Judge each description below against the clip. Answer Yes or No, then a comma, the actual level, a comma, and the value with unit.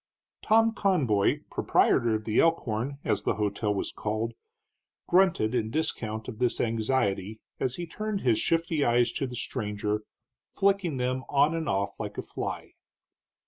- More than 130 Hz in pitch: No, low, 125 Hz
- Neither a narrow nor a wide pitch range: No, wide, 6.9 semitones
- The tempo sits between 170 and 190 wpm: No, average, 150 wpm